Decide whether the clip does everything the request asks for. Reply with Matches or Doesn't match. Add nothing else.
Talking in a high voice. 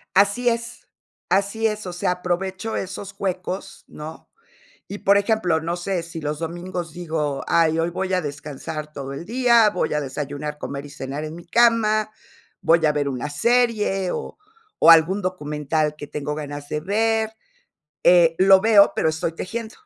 Doesn't match